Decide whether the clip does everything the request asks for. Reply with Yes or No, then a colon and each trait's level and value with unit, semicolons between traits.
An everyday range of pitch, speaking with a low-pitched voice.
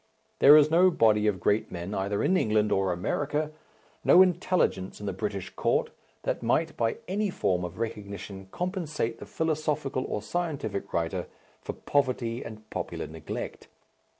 No: wide, 7.6 semitones; low, 115 Hz